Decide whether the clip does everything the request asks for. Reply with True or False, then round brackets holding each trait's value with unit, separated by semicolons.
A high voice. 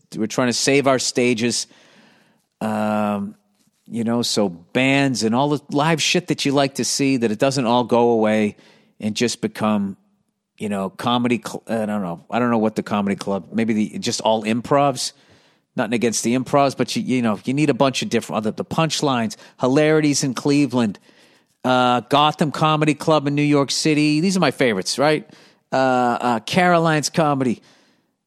False (125 Hz)